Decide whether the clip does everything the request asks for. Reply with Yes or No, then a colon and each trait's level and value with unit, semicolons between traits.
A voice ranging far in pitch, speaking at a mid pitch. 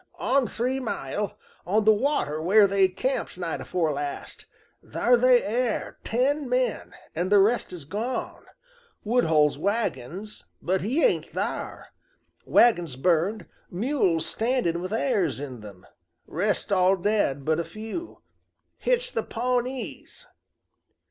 No: wide, 6.6 semitones; high, 205 Hz